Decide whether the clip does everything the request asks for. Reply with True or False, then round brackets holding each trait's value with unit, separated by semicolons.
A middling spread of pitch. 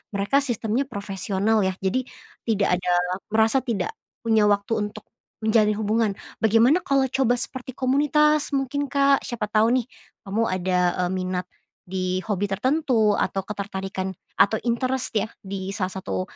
True (4.9 semitones)